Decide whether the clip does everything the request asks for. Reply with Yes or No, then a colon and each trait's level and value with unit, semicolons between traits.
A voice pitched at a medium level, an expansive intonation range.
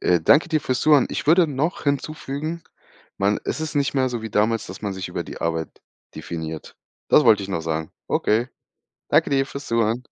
No: low, 120 Hz; wide, 6.8 semitones